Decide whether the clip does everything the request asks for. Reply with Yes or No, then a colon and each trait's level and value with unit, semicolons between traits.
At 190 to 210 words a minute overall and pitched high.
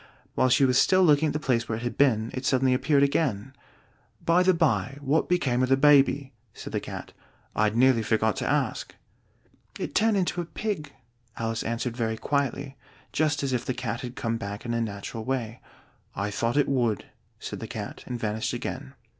No: average, 195 wpm; low, 130 Hz